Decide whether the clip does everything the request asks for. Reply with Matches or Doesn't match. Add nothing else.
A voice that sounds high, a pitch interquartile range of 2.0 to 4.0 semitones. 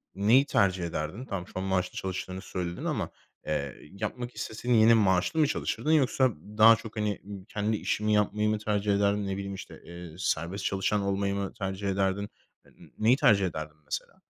Doesn't match